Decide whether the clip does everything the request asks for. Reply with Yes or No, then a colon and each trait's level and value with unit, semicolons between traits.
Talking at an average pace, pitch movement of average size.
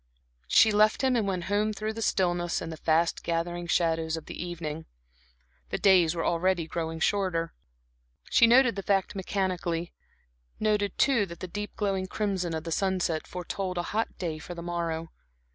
Yes: average, 175 wpm; average, 3.4 semitones